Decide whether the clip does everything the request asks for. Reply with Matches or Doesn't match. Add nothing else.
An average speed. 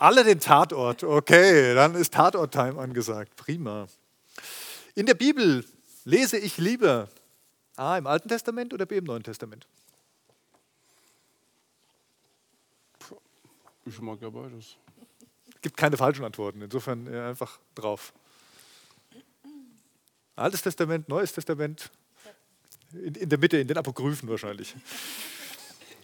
Doesn't match